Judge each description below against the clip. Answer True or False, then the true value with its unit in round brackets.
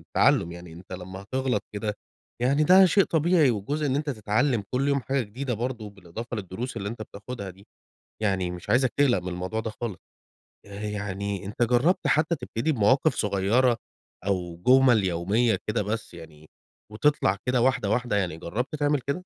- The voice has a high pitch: False (110 Hz)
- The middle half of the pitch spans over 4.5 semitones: True (5.0 semitones)